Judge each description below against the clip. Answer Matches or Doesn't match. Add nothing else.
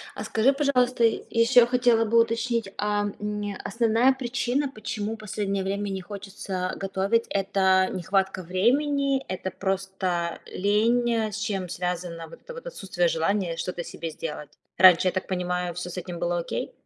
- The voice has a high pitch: Matches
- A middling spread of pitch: Matches